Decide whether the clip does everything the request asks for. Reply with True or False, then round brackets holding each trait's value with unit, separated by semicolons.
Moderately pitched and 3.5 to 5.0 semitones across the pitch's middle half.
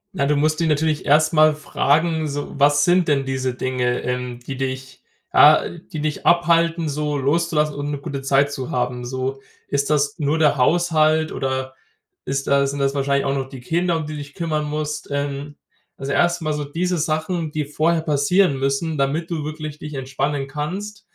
False (150 Hz; 2.5 semitones)